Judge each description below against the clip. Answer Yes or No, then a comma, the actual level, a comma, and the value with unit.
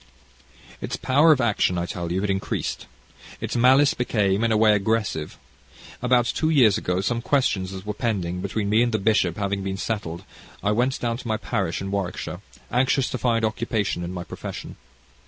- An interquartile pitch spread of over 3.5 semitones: Yes, average, 3.9 semitones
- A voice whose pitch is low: Yes, low, 105 Hz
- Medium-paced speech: Yes, average, 190 wpm